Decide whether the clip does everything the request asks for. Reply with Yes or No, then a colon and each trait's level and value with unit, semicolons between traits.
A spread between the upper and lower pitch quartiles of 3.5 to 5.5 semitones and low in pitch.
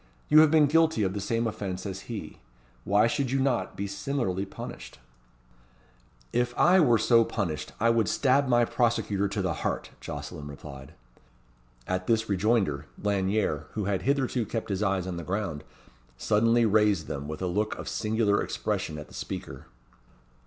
Yes: average, 4.1 semitones; low, 105 Hz